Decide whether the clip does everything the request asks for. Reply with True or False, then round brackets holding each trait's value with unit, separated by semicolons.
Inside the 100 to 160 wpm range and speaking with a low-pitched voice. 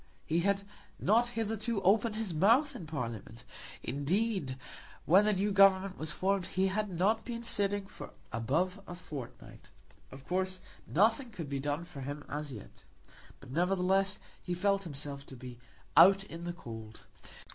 False (155 wpm; 185 Hz)